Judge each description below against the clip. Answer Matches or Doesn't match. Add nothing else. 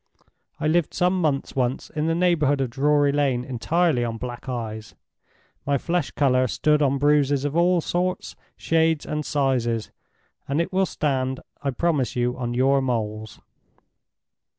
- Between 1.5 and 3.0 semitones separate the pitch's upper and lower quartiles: Doesn't match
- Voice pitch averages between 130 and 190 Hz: Matches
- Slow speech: Doesn't match